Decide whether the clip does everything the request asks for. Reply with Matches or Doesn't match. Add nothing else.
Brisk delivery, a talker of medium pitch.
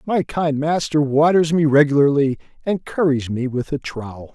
Doesn't match